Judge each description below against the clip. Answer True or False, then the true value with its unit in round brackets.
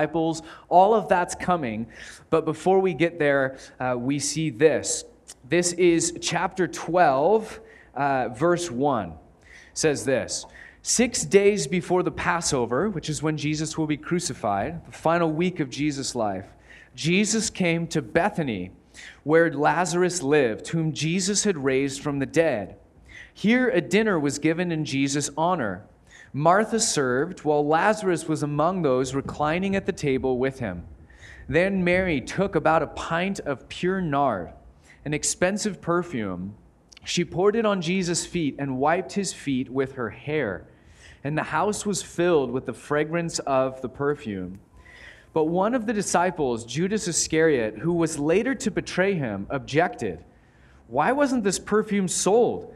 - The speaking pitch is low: False (160 Hz)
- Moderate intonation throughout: True (4.8 semitones)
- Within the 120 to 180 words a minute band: True (150 wpm)